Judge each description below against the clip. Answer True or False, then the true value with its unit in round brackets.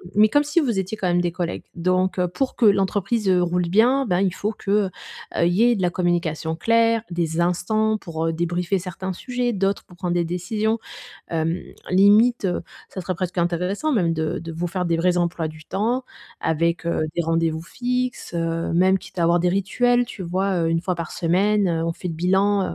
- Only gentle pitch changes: False (3.5 semitones)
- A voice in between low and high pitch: True (180 Hz)